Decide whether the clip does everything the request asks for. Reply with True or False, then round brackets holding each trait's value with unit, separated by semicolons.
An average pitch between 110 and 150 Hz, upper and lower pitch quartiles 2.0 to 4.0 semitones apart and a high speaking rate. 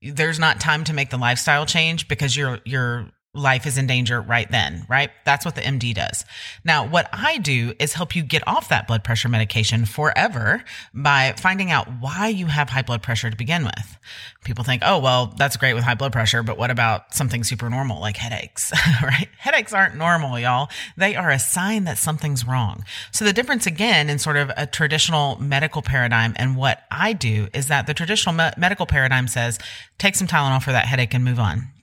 False (135 Hz; 4.5 semitones; 210 wpm)